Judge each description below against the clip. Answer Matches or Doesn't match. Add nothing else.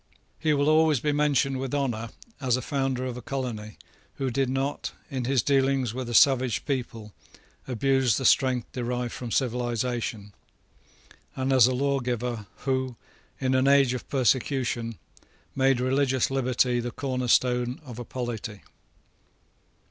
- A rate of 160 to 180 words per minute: Doesn't match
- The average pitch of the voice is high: Doesn't match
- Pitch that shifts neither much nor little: Doesn't match